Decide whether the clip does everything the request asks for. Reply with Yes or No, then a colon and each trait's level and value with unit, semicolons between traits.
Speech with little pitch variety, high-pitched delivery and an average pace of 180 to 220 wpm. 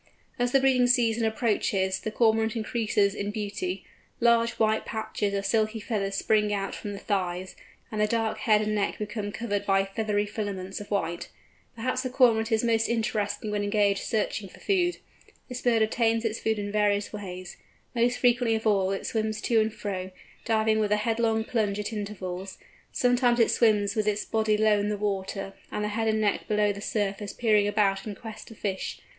Yes: narrow, 1.8 semitones; high, 215 Hz; average, 190 wpm